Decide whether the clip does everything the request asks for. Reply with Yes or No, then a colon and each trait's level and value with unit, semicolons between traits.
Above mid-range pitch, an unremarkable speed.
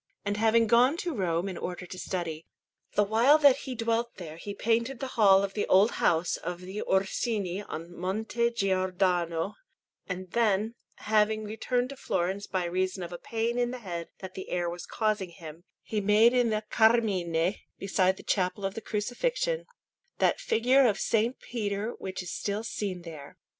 Yes: high, 200 Hz; average, 180 wpm